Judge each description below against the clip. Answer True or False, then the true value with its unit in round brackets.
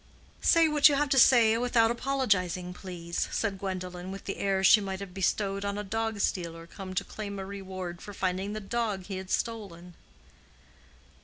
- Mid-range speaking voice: False (195 Hz)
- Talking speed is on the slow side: False (180 wpm)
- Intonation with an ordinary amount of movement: True (3.2 semitones)